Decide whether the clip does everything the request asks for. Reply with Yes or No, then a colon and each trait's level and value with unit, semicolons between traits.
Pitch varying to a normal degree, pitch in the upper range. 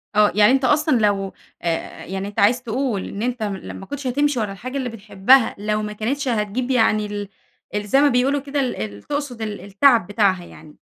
Yes: average, 4.3 semitones; high, 220 Hz